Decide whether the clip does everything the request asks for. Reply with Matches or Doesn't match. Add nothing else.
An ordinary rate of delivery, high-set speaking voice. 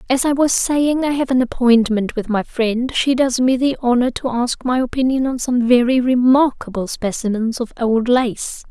Matches